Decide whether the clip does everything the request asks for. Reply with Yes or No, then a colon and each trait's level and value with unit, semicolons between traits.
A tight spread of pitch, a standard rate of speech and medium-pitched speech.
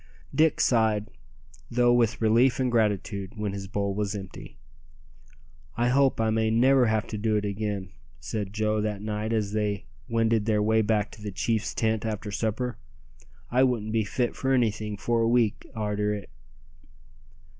No: narrow, 1.9 semitones; average, 165 wpm; low, 110 Hz